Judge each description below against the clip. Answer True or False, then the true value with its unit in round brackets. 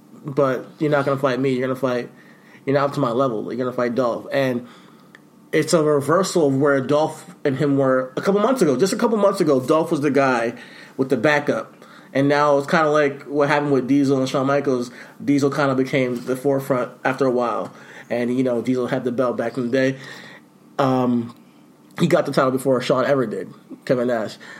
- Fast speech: True (215 wpm)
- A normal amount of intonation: False (2.3 semitones)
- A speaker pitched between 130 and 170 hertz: True (135 Hz)